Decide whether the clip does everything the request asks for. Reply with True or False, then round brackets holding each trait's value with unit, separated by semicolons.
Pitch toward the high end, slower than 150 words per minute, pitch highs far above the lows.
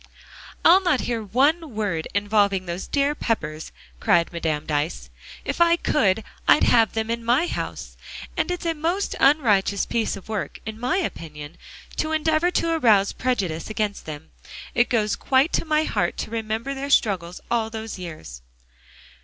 False (220 Hz; 160 wpm; 7.5 semitones)